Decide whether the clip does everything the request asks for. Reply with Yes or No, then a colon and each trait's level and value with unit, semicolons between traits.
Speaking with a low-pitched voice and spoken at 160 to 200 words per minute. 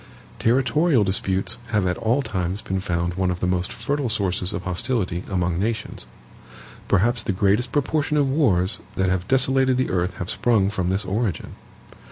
Yes: low, 100 Hz; average, 170 wpm